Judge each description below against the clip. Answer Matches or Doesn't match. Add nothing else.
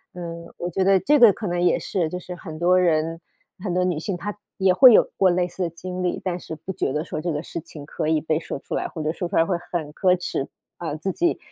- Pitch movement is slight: Matches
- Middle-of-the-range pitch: Matches